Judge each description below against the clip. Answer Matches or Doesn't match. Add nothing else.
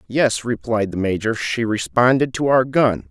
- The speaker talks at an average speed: Matches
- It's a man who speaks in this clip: Matches